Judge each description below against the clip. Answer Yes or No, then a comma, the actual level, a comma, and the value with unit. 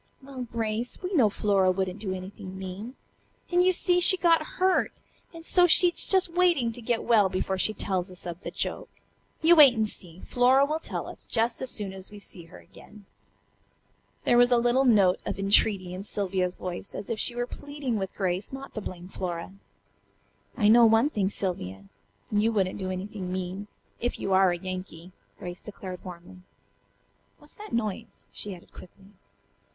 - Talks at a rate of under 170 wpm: No, average, 185 wpm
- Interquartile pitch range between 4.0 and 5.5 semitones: Yes, average, 4.8 semitones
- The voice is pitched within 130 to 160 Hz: No, high, 205 Hz